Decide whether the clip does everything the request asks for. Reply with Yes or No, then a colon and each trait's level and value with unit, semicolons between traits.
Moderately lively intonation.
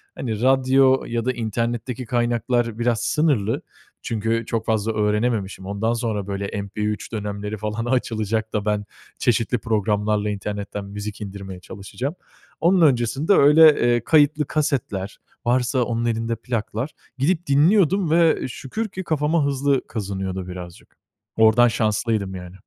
Yes: average, 4.0 semitones